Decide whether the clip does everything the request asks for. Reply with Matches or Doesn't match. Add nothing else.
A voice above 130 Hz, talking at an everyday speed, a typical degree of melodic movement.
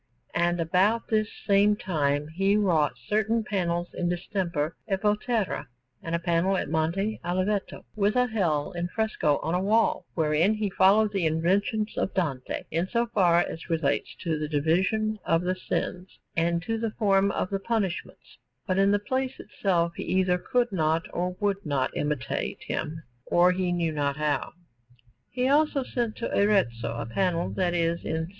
Matches